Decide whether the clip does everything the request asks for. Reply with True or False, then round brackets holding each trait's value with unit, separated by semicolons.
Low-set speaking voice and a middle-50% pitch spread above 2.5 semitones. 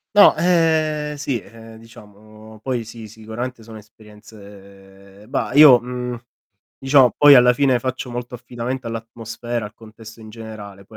True (115 Hz; 2.9 semitones)